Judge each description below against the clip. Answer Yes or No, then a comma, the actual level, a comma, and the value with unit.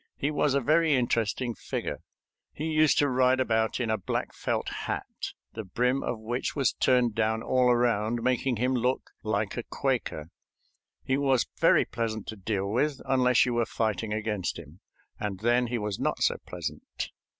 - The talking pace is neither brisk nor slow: Yes, average, 175 wpm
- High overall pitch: No, low, 120 Hz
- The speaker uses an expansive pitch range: No, average, 2.9 semitones